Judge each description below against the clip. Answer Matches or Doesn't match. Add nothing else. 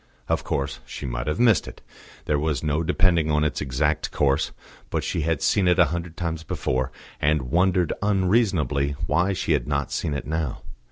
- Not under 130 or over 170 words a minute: Doesn't match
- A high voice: Doesn't match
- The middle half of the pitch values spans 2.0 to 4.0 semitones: Matches